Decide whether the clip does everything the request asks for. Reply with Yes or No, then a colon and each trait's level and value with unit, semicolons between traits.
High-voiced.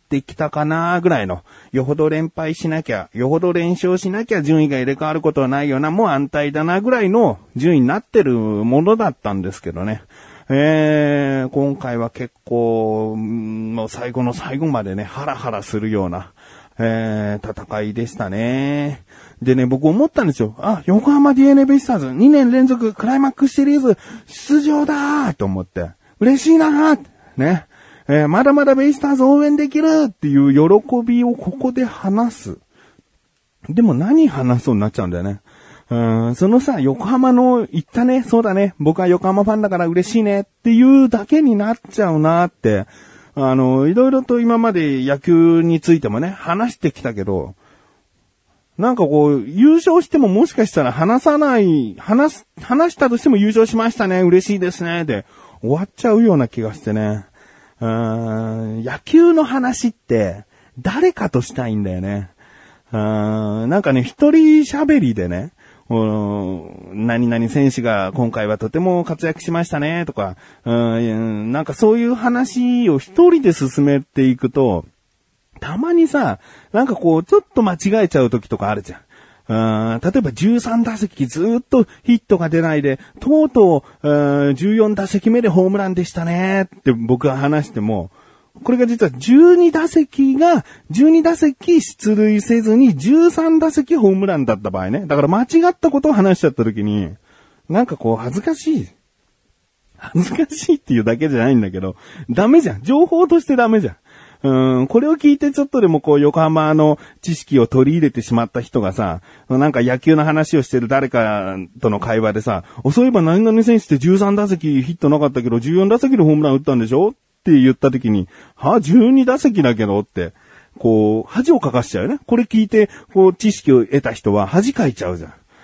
No: medium, 160 Hz